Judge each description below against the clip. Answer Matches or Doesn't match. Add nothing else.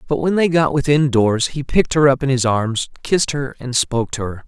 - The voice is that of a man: Matches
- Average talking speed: Doesn't match